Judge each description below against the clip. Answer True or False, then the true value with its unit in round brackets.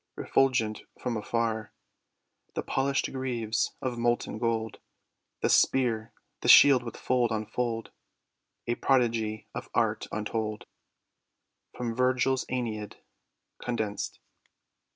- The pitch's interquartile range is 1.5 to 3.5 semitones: True (2.5 semitones)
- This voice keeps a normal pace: False (105 wpm)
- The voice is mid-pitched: False (115 Hz)